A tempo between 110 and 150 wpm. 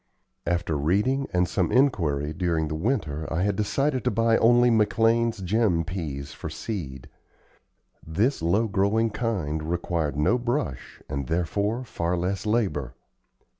Yes: slow, 135 wpm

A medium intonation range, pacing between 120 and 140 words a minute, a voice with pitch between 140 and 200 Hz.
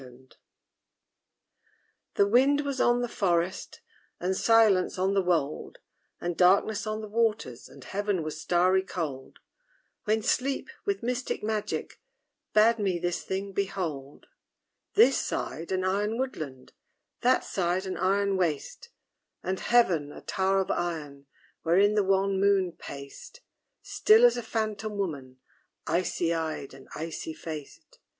Yes: average, 4.5 semitones; slow, 135 wpm; high, 190 Hz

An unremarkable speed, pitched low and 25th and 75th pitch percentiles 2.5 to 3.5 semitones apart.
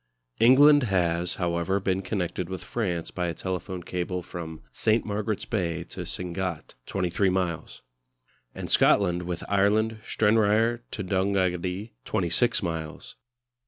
No: slow, 125 wpm; very low, 95 Hz; average, 3.1 semitones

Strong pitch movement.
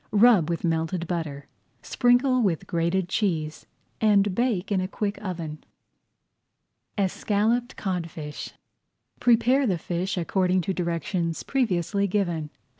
No: average, 3.8 semitones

